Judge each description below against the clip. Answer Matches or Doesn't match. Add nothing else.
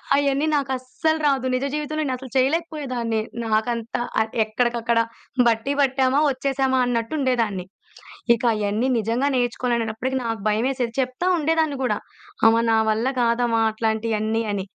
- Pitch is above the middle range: Matches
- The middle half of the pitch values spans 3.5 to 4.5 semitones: Doesn't match